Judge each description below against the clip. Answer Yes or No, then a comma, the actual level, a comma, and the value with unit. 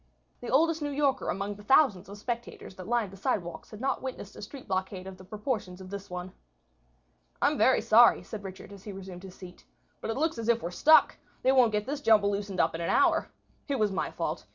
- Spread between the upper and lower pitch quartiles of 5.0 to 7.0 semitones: Yes, average, 5.3 semitones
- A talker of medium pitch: No, high, 205 Hz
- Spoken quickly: Yes, fast, 235 wpm